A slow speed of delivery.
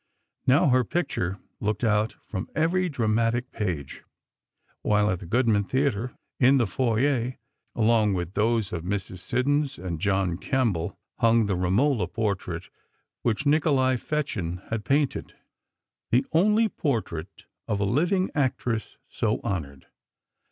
Yes: slow, 130 wpm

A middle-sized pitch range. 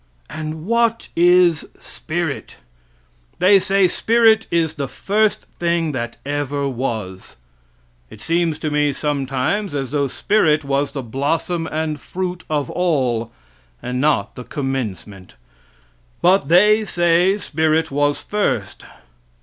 Yes: average, 4.6 semitones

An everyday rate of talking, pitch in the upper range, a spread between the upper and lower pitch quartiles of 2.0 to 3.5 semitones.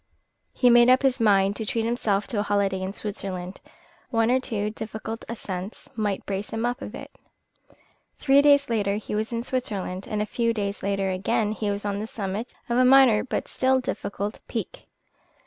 Yes: average, 190 wpm; high, 215 Hz; average, 3.0 semitones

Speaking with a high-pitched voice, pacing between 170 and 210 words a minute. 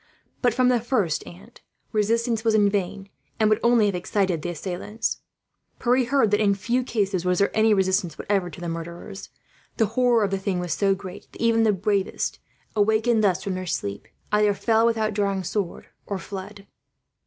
Yes: high, 205 Hz; average, 190 wpm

